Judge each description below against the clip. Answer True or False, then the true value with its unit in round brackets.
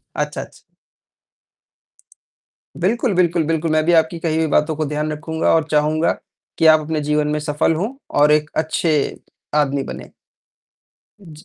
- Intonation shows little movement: True (1.5 semitones)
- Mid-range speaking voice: True (155 Hz)